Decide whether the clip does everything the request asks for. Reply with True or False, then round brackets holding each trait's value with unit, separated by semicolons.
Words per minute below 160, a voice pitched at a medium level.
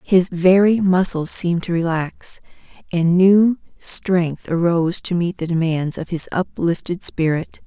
True (140 wpm; 175 Hz)